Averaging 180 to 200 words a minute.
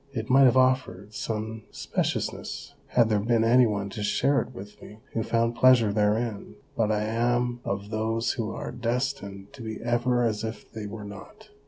Yes: average, 185 wpm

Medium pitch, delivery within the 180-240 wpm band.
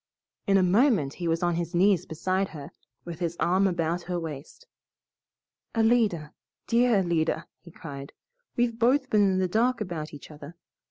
No: medium, 180 Hz; average, 165 wpm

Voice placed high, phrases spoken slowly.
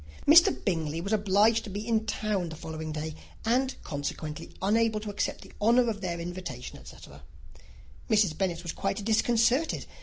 No: high, 200 Hz; average, 160 wpm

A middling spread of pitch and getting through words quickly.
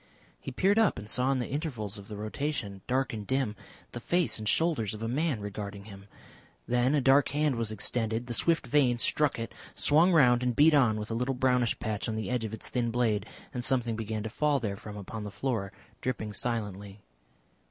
Yes: average, 3.9 semitones; fast, 210 wpm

